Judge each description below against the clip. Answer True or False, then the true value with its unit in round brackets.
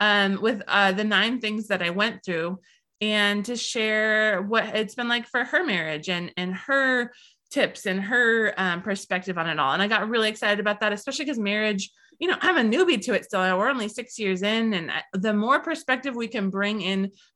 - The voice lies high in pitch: True (215 Hz)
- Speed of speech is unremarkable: False (210 wpm)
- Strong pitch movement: False (3.4 semitones)